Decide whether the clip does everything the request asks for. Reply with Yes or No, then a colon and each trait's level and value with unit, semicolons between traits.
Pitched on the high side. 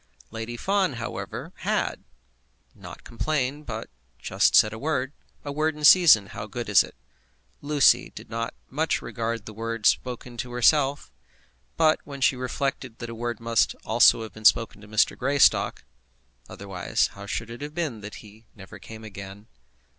No: low, 115 Hz